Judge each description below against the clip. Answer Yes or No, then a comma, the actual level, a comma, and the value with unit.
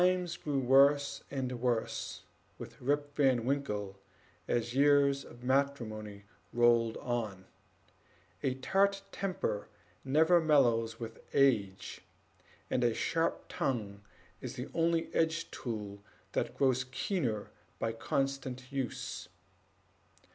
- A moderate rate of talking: No, slow, 110 wpm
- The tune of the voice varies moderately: Yes, average, 3.8 semitones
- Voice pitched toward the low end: Yes, low, 130 Hz